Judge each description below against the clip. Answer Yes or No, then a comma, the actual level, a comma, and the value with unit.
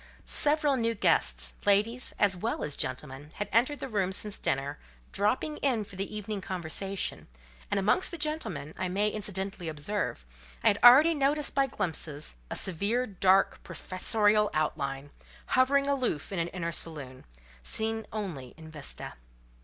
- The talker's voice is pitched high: Yes, high, 200 Hz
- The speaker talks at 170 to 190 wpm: No, average, 150 wpm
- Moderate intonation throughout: No, wide, 6.5 semitones